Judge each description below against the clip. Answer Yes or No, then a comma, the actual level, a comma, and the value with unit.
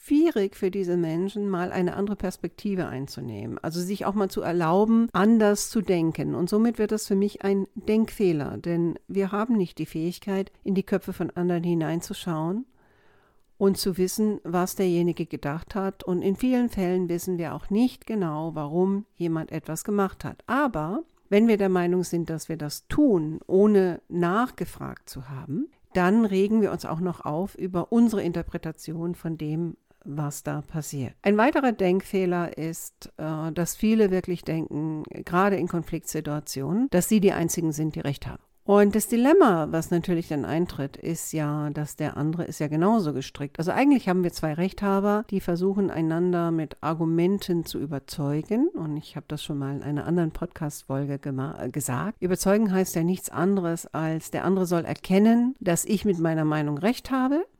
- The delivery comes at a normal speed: Yes, average, 170 wpm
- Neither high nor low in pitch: Yes, medium, 175 Hz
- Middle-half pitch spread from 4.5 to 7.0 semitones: No, average, 3.9 semitones